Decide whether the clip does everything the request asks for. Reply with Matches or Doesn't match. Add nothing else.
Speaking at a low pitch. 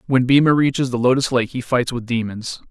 Matches